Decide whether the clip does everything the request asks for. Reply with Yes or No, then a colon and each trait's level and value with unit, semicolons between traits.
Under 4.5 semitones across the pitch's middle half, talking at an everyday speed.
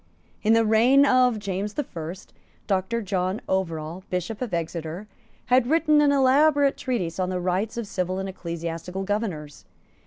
No: wide, 5.5 semitones; average, 155 wpm